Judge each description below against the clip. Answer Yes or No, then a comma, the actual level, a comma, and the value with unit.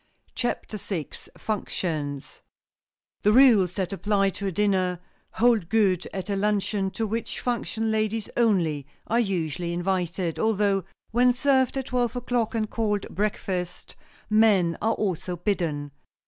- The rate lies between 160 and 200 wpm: No, slow, 135 wpm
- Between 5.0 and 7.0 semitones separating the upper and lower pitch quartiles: No, average, 3.8 semitones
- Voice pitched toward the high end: Yes, high, 200 Hz